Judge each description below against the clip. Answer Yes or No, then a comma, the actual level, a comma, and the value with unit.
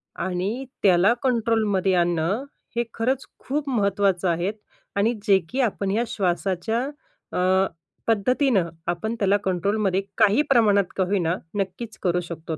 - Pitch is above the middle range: Yes, high, 200 Hz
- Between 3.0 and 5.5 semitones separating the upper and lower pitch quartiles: Yes, average, 3.7 semitones